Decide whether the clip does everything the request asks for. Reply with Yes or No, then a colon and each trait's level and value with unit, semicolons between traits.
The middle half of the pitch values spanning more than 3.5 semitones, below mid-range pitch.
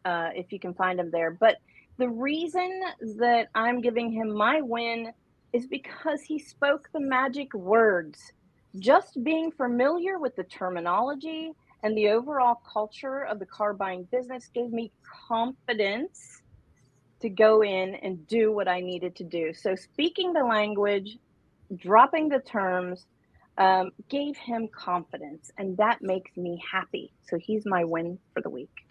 No: wide, 5.6 semitones; high, 220 Hz